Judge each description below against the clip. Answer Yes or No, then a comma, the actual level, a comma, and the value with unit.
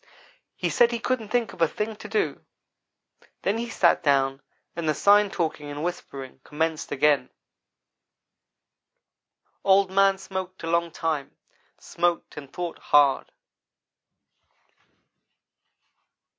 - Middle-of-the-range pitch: Yes, medium, 170 Hz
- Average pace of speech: No, slow, 115 wpm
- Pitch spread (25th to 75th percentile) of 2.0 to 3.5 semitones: No, average, 5.2 semitones